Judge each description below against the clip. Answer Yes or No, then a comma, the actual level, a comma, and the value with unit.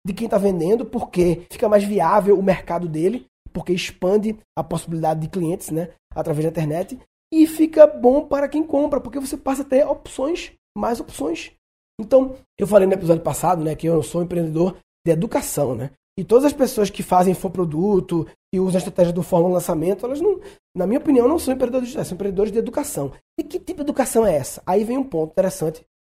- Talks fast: Yes, fast, 205 wpm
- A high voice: Yes, high, 195 Hz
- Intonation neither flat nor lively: No, wide, 7.1 semitones